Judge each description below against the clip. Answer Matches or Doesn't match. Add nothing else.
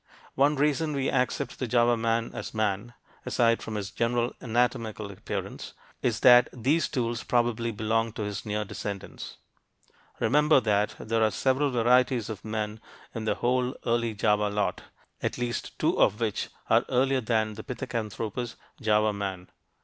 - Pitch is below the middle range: Matches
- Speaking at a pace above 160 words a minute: Doesn't match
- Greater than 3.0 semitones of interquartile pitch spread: Doesn't match